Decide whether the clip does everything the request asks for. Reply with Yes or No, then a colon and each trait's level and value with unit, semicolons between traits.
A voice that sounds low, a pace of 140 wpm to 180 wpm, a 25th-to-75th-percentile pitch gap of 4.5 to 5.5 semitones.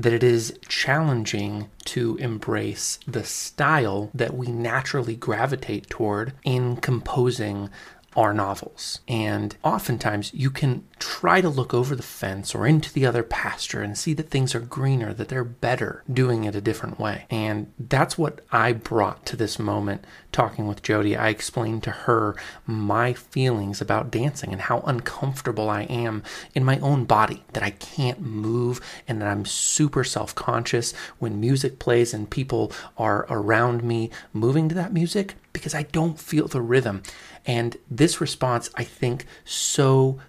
No: low, 120 Hz; average, 160 wpm; average, 3.6 semitones